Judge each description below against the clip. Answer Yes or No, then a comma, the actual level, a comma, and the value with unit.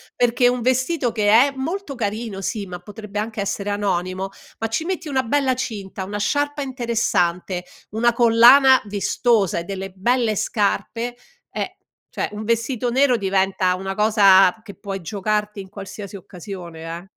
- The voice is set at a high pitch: Yes, high, 210 Hz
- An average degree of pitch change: Yes, average, 3.9 semitones